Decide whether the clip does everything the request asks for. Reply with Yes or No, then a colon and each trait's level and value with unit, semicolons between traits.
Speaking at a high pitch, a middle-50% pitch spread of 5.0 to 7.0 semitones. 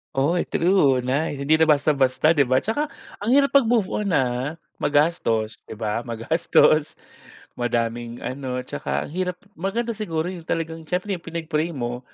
No: medium, 155 Hz; wide, 5.5 semitones